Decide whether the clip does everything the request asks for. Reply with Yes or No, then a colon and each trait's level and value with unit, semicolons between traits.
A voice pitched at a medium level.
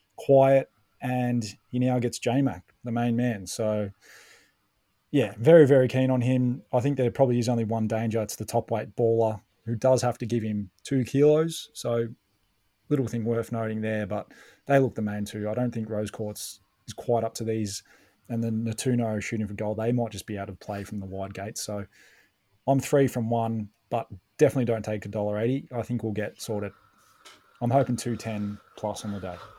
No: low, 115 Hz